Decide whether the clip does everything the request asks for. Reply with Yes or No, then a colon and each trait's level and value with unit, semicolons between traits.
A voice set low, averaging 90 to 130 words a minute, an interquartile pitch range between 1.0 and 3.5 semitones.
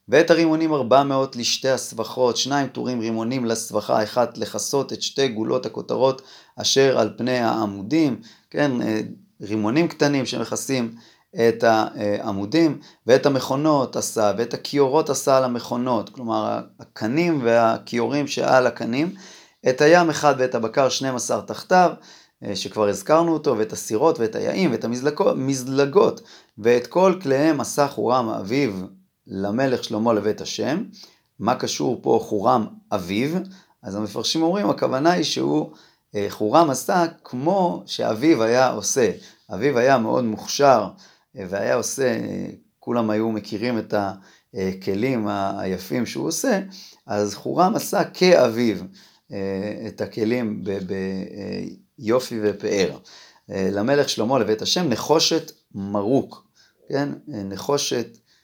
No: low, 120 Hz; average, 120 wpm; average, 5.2 semitones